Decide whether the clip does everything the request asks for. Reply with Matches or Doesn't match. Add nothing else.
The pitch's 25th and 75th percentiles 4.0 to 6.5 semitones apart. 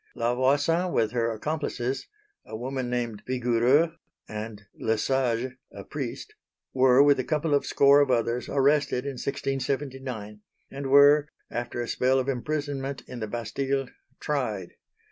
Doesn't match